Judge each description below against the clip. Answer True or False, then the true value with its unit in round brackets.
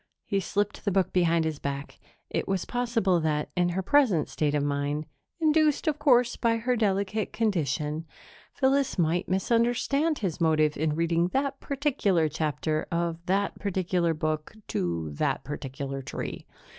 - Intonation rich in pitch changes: True (6.9 semitones)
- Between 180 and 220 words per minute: False (150 wpm)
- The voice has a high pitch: False (180 Hz)